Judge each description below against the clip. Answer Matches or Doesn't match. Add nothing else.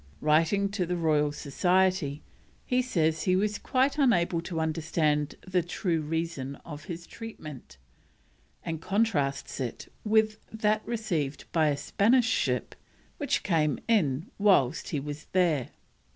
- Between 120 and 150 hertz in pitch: Doesn't match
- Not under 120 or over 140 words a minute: Matches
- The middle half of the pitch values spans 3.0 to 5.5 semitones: Matches